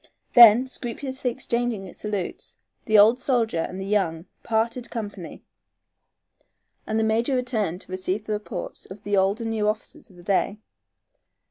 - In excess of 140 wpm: Yes, average, 150 wpm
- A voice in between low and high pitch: No, high, 215 Hz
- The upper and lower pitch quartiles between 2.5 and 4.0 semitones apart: Yes, average, 3.4 semitones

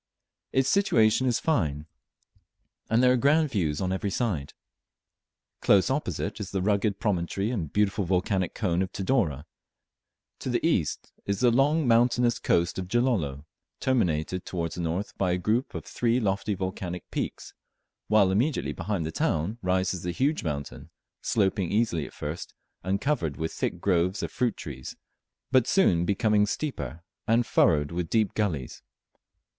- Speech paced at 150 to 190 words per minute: Yes, average, 155 wpm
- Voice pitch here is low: Yes, low, 100 Hz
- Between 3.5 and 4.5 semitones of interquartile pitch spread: No, wide, 5.5 semitones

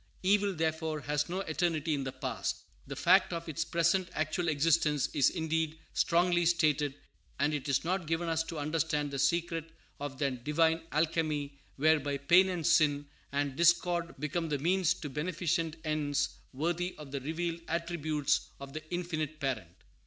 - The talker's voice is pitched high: No, medium, 160 Hz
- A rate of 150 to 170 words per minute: Yes, average, 160 wpm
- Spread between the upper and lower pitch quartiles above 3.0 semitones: No, average, 2.7 semitones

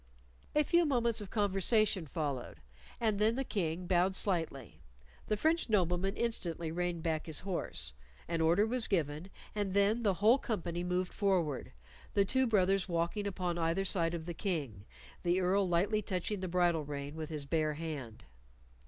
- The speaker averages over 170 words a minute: No, average, 165 wpm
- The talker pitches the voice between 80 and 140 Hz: No, medium, 180 Hz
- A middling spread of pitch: Yes, average, 3.9 semitones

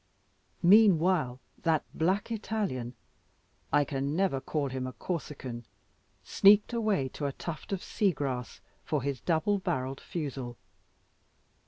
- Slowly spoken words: Yes, slow, 125 wpm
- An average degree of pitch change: No, wide, 6.3 semitones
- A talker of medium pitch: Yes, medium, 150 Hz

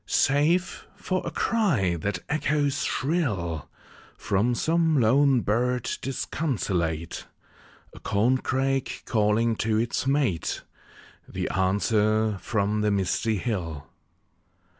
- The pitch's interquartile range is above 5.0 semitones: Yes, wide, 5.4 semitones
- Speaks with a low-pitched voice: Yes, low, 115 Hz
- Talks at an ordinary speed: No, slow, 95 wpm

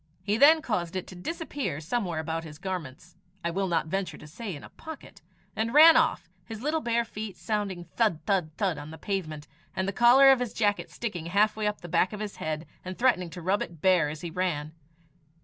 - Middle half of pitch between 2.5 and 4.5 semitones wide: No, average, 5.2 semitones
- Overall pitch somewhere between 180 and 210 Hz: Yes, high, 190 Hz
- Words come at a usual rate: No, fast, 220 wpm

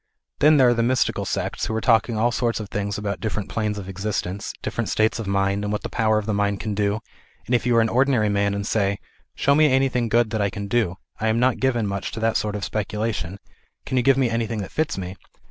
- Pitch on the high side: No, low, 110 Hz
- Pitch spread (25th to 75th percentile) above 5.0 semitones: No, average, 2.8 semitones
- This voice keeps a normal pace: No, fast, 260 wpm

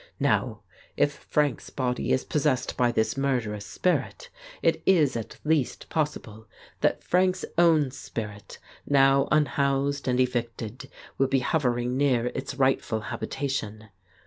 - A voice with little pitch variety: No, average, 3.1 semitones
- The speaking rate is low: Yes, slow, 130 wpm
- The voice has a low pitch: Yes, low, 130 Hz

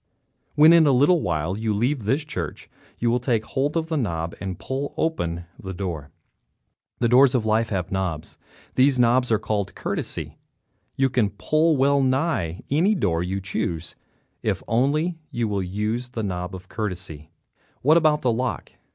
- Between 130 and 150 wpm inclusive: No, average, 170 wpm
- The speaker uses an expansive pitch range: Yes, wide, 6.9 semitones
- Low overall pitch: Yes, low, 115 Hz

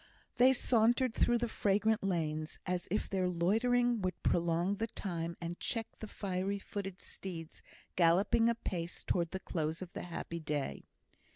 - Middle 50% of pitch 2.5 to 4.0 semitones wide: No, average, 4.5 semitones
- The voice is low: No, medium, 185 Hz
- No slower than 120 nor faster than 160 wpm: Yes, average, 155 wpm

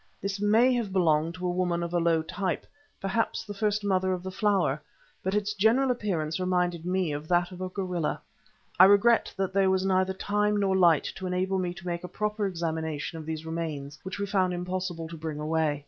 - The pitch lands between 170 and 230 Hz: Yes, medium, 185 Hz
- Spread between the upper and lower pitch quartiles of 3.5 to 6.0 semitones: No, average, 2.9 semitones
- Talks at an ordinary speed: No, fast, 215 wpm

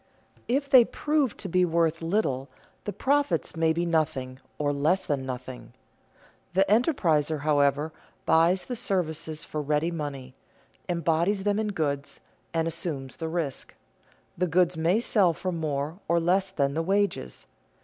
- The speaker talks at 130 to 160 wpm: Yes, average, 150 wpm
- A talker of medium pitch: Yes, medium, 165 Hz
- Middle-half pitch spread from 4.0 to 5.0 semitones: Yes, average, 4.4 semitones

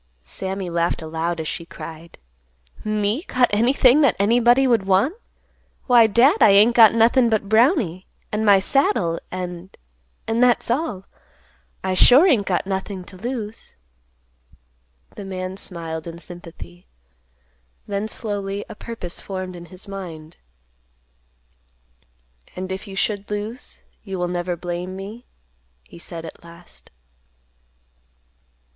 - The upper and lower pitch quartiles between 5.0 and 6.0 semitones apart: No, average, 4.5 semitones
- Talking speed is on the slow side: Yes, slow, 125 wpm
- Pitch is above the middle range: Yes, high, 195 Hz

